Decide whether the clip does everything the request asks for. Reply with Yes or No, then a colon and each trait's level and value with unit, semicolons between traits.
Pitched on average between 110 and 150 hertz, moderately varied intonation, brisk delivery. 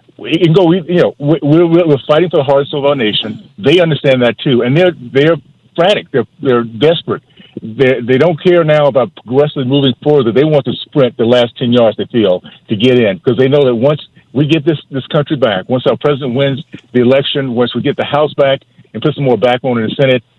Yes: medium, 140 Hz; average, 3.5 semitones; fast, 235 wpm